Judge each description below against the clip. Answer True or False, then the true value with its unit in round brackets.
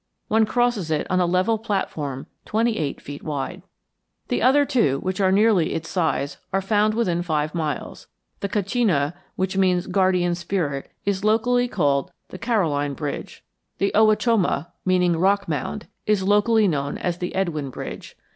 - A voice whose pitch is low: False (185 Hz)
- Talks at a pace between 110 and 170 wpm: True (155 wpm)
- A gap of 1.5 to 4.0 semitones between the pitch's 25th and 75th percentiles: False (4.9 semitones)